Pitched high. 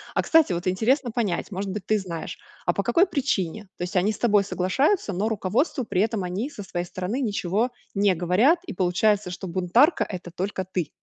Yes: high, 200 Hz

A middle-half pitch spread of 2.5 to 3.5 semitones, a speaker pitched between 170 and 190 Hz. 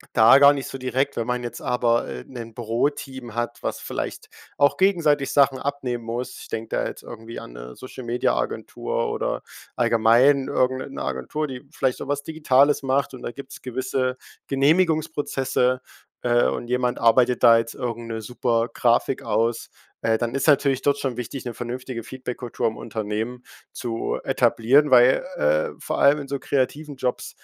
No: average, 2.9 semitones; low, 125 Hz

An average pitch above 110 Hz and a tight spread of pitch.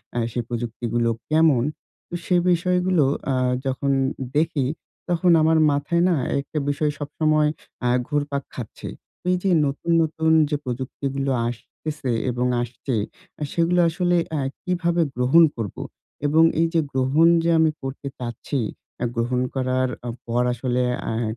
No: medium, 140 Hz; average, 4.5 semitones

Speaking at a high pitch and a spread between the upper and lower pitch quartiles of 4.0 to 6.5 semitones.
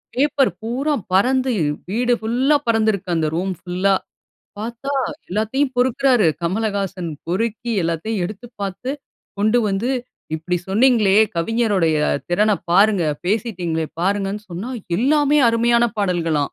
Yes: high, 215 Hz; average, 4.5 semitones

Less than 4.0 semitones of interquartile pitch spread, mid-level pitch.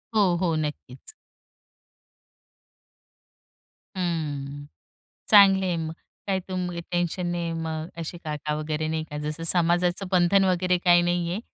Yes: narrow, 2.4 semitones; medium, 170 Hz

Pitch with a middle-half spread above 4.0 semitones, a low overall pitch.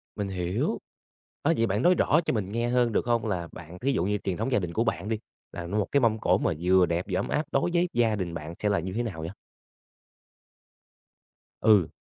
Yes: average, 4.6 semitones; low, 105 Hz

